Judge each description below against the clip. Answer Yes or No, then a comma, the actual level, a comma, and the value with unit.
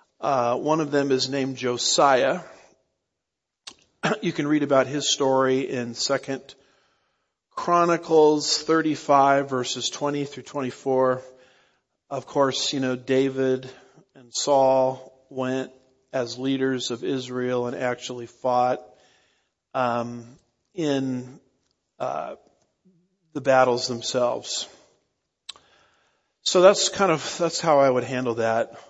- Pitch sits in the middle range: No, low, 130 Hz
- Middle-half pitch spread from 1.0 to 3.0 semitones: Yes, narrow, 2.5 semitones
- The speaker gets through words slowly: Yes, slow, 110 wpm